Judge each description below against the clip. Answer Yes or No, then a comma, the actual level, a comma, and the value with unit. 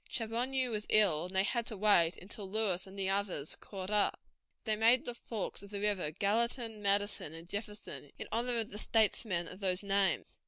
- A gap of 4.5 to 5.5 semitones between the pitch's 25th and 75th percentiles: No, average, 2.8 semitones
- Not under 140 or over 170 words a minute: No, average, 195 wpm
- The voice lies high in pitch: Yes, high, 205 Hz